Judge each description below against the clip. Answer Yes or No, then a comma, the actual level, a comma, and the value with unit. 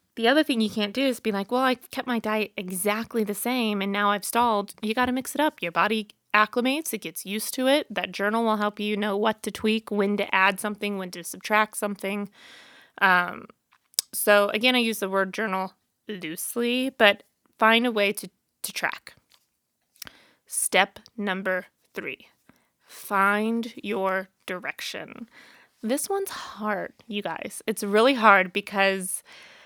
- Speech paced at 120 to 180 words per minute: Yes, average, 170 wpm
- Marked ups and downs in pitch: No, average, 3.2 semitones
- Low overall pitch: No, high, 215 Hz